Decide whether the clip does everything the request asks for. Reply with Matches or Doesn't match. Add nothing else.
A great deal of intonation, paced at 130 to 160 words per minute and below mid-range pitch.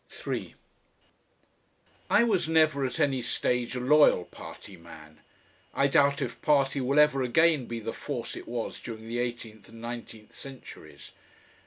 Doesn't match